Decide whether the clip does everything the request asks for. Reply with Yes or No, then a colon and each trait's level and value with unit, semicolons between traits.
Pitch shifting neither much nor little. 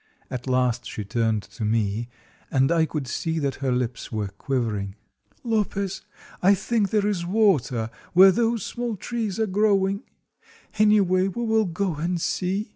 No: wide, 8.7 semitones